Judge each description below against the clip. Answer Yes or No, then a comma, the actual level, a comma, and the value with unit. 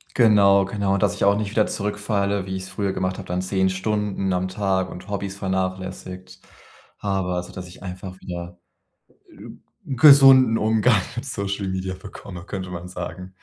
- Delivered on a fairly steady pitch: Yes, narrow, 1.8 semitones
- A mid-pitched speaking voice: No, very low, 95 Hz